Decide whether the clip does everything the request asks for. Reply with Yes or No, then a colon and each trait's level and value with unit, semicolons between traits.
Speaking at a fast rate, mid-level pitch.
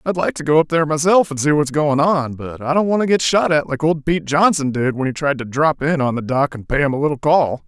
Yes: fast, 315 wpm; medium, 150 Hz